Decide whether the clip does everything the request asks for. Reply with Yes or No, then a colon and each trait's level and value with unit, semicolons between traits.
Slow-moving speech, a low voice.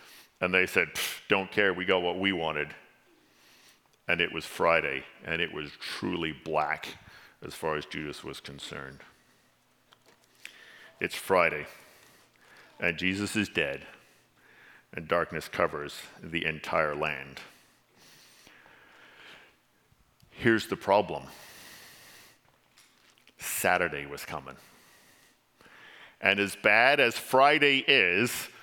Yes: slow, 105 wpm; very low, 90 Hz